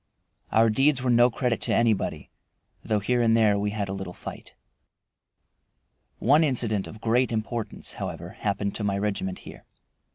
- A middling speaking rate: Yes, average, 160 wpm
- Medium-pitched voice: No, low, 110 Hz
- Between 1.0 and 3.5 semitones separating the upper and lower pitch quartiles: Yes, average, 2.9 semitones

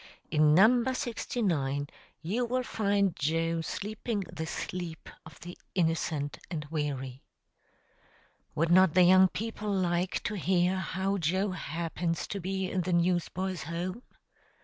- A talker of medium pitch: Yes, medium, 180 Hz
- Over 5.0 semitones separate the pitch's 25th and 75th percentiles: No, average, 3.1 semitones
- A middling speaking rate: No, slow, 130 wpm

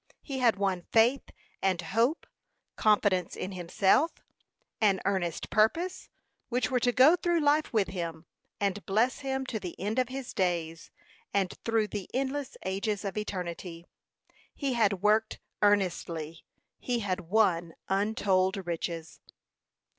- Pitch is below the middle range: No, high, 205 Hz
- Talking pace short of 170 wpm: Yes, slow, 135 wpm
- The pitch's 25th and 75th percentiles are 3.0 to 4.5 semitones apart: No, average, 5.0 semitones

